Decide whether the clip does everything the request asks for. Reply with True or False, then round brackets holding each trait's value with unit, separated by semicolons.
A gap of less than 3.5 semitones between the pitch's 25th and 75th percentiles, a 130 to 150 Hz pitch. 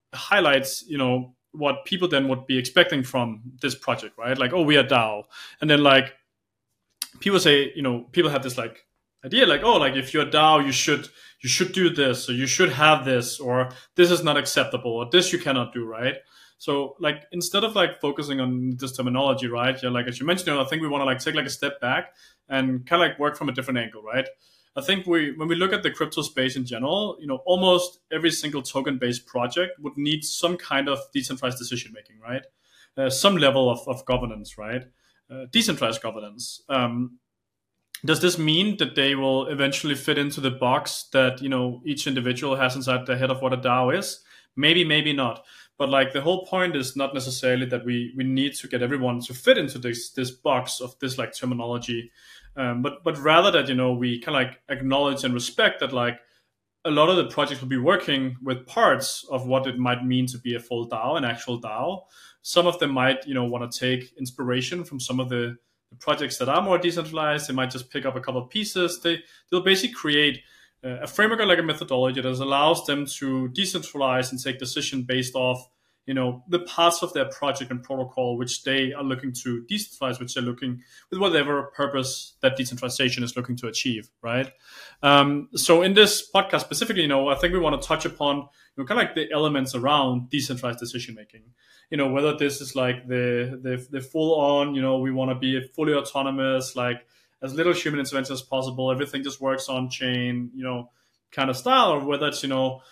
True (2.9 semitones; 135 Hz)